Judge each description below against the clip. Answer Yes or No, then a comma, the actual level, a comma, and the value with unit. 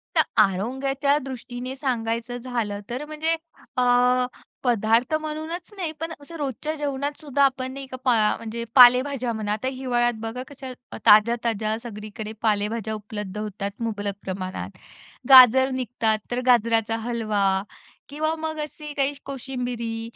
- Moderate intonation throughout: Yes, average, 3.7 semitones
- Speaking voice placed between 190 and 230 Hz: No, high, 245 Hz